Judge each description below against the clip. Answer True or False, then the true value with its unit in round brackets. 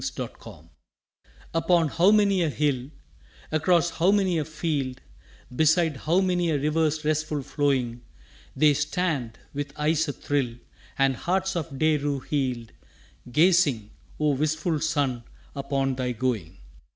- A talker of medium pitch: True (150 Hz)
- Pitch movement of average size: True (3.5 semitones)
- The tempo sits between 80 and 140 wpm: True (135 wpm)